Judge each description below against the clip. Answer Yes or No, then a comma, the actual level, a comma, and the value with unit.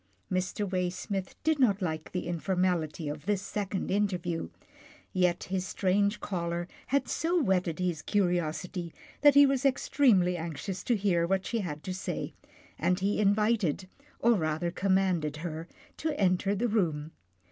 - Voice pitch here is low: No, medium, 185 Hz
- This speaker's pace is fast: No, average, 150 wpm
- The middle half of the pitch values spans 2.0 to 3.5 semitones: Yes, average, 3.1 semitones